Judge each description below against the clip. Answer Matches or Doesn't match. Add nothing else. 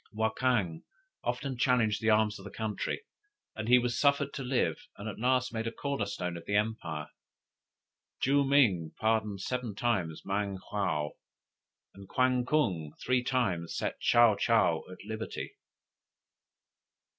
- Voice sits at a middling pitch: Doesn't match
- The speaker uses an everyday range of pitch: Matches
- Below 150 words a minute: Matches